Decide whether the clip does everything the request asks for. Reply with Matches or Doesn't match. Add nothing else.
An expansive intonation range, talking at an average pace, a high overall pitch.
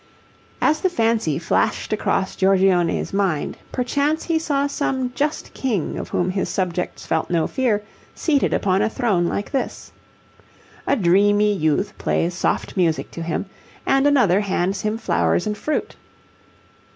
Matches